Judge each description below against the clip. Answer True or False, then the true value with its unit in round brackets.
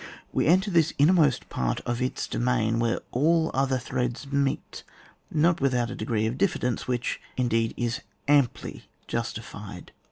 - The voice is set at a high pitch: False (125 Hz)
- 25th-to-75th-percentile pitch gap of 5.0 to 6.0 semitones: False (3.6 semitones)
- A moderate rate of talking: True (155 wpm)